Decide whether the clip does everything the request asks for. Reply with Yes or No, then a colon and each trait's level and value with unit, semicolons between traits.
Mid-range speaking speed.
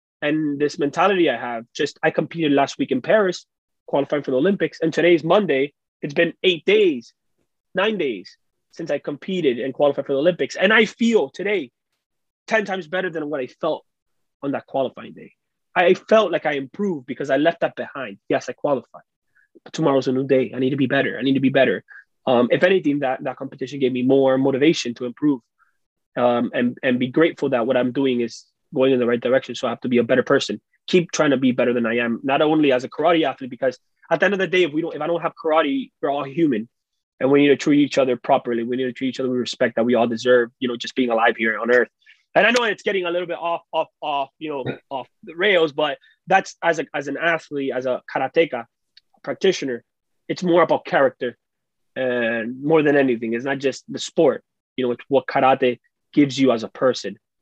No: fast, 230 wpm